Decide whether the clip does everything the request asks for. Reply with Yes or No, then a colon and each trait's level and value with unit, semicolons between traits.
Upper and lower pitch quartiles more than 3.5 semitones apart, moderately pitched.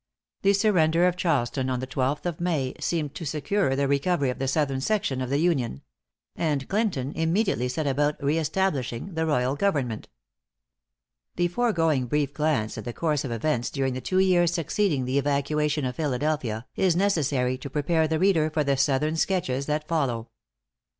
Yes: average, 4.1 semitones; medium, 150 Hz